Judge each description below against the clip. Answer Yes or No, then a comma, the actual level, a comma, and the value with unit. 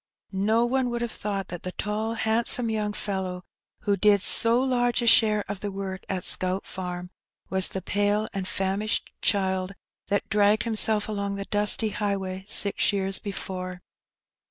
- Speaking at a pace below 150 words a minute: No, average, 160 wpm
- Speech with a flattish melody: Yes, narrow, 2.2 semitones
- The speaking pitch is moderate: No, high, 205 Hz